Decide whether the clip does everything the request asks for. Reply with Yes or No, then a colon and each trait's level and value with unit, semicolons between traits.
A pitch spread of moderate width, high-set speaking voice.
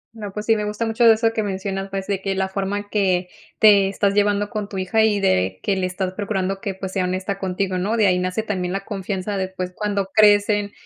No: narrow, 1.7 semitones; high, 195 Hz